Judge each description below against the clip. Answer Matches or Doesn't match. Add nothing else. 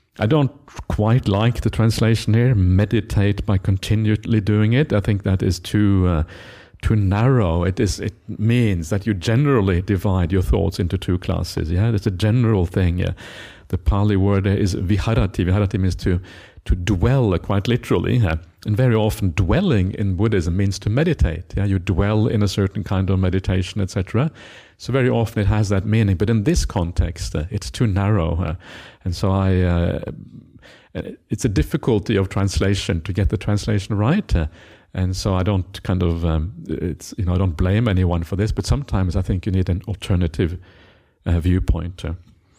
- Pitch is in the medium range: Doesn't match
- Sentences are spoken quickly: Doesn't match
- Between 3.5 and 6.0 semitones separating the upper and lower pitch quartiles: Doesn't match